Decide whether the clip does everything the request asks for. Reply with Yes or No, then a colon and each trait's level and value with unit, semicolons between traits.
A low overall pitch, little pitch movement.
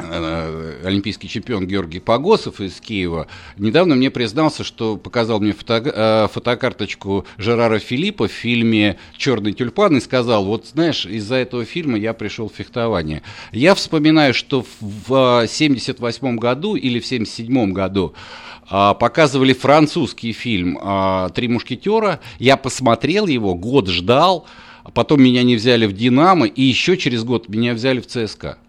No: low, 115 Hz; average, 4.2 semitones